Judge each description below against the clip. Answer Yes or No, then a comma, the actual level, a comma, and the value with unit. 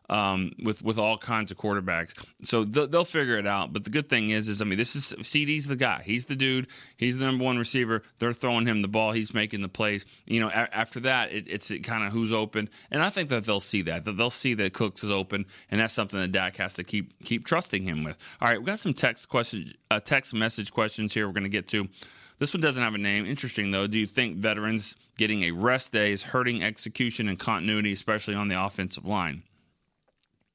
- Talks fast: Yes, fast, 240 wpm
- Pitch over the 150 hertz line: No, low, 110 Hz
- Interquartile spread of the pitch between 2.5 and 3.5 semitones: Yes, average, 2.9 semitones